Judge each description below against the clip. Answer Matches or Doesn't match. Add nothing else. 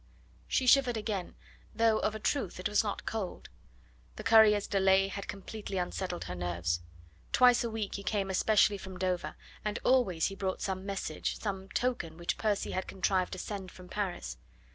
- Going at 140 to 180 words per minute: Matches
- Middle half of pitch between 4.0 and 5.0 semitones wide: Doesn't match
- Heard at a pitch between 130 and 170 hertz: Doesn't match